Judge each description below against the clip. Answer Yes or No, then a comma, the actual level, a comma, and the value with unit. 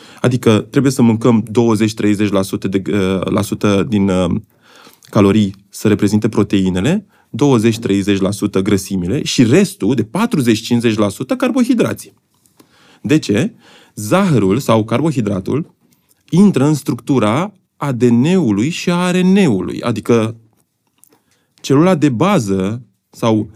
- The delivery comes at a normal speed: No, slow, 100 wpm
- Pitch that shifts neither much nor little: No, wide, 6.3 semitones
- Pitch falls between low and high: No, low, 115 Hz